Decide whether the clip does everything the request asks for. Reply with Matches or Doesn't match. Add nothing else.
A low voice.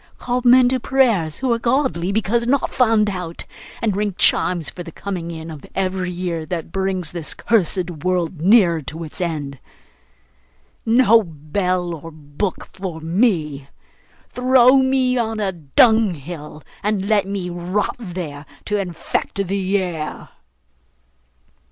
Doesn't match